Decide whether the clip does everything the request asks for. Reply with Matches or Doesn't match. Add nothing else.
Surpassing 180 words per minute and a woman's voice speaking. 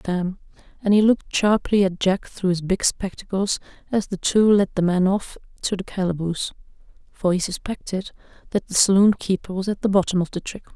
Matches